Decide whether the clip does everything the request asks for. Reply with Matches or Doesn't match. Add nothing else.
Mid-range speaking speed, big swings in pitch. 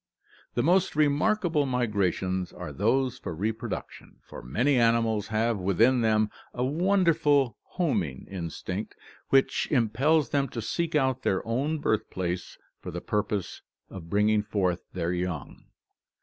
Doesn't match